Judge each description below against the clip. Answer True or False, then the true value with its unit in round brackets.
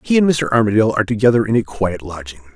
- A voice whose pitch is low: True (110 Hz)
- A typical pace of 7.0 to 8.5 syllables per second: True (7.4 syllables/s)